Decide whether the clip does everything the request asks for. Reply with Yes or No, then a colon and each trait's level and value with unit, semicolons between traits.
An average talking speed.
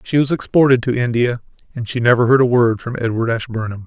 No: fast, 215 wpm